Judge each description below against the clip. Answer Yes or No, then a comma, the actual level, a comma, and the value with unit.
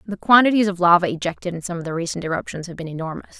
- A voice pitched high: No, medium, 180 Hz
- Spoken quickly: Yes, fast, 245 wpm